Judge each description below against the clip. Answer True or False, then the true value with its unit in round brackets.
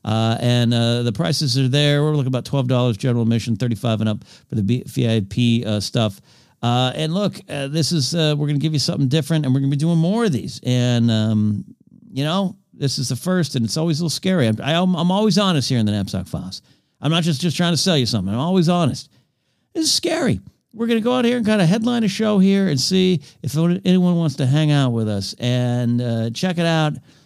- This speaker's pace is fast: True (245 wpm)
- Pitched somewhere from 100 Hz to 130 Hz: False (140 Hz)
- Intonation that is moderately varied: False (6.1 semitones)